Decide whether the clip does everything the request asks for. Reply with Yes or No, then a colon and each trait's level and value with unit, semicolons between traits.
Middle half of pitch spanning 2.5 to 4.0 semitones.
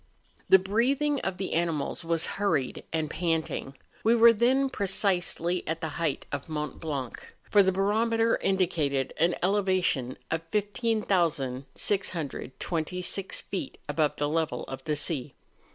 No: average, 4.8 semitones